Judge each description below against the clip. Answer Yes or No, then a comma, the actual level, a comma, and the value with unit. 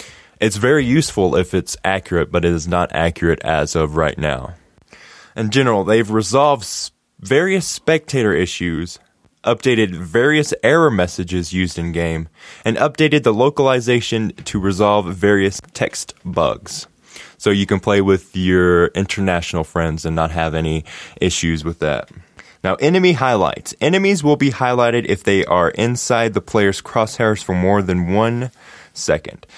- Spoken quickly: No, average, 145 wpm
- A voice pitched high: No, low, 100 Hz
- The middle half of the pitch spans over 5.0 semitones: Yes, wide, 5.5 semitones